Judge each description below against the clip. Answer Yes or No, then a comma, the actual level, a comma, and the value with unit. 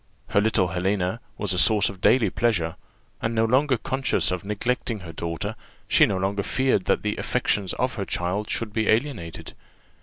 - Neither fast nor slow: Yes, average, 180 wpm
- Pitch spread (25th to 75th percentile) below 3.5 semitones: No, average, 3.8 semitones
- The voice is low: Yes, low, 105 Hz